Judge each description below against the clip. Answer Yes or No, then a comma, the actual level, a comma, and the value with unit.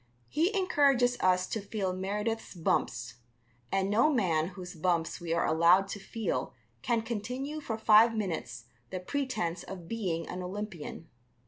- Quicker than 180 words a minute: No, average, 145 wpm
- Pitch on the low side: No, high, 195 Hz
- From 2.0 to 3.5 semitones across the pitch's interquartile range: No, average, 4.4 semitones